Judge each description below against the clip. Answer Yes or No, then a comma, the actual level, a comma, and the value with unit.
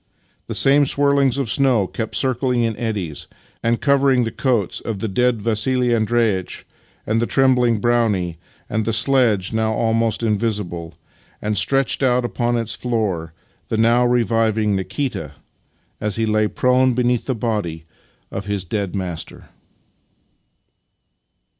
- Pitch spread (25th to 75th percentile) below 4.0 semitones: Yes, average, 3.0 semitones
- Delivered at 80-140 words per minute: Yes, slow, 135 wpm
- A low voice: Yes, low, 115 Hz